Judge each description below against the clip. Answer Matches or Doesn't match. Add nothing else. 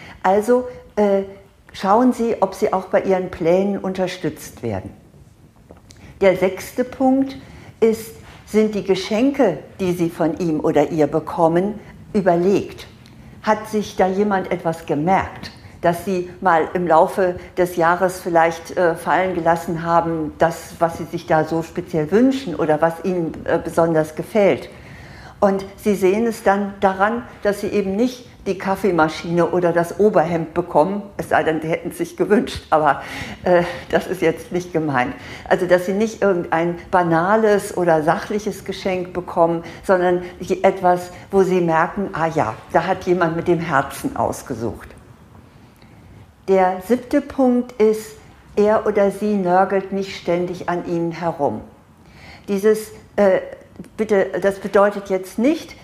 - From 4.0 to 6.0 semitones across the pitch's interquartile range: Doesn't match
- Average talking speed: Matches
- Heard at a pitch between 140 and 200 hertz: Matches